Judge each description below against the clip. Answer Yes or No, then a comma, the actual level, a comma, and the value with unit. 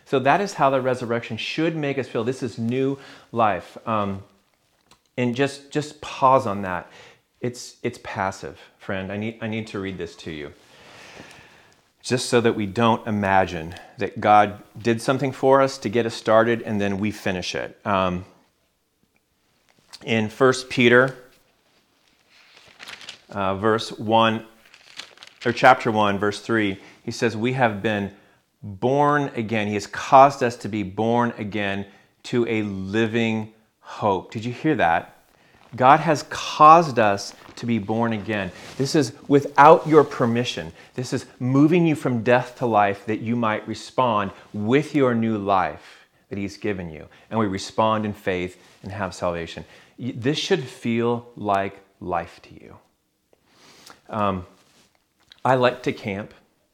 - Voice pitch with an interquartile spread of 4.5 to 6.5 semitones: No, average, 3.7 semitones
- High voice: No, low, 115 Hz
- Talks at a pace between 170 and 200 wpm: No, average, 150 wpm